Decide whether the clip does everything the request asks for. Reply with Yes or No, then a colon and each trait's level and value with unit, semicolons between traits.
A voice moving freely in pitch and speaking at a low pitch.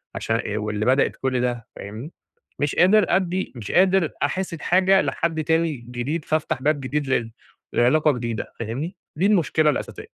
No: wide, 5.8 semitones; medium, 150 Hz